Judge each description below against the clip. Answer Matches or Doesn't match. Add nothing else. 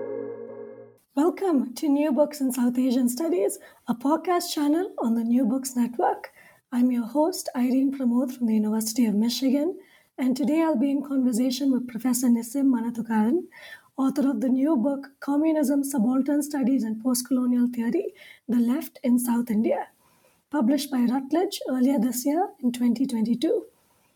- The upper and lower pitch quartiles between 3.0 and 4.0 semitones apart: Matches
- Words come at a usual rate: Matches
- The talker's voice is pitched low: Doesn't match